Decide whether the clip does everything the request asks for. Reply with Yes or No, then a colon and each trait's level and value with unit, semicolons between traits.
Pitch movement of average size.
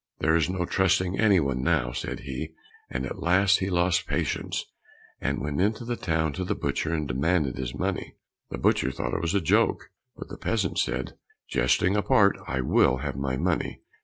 No: wide, 5.7 semitones